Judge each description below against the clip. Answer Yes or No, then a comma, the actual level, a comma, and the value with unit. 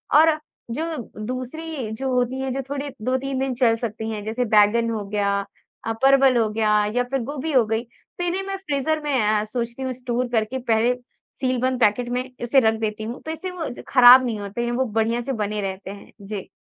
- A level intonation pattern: No, average, 3.3 semitones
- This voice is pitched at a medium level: No, high, 245 Hz